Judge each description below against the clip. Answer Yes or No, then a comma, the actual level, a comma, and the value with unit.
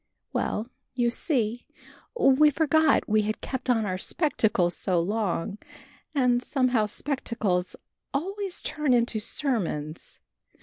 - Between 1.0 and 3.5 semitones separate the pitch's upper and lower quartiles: No, average, 4.9 semitones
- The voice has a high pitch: Yes, high, 240 Hz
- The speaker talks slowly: Yes, slow, 115 wpm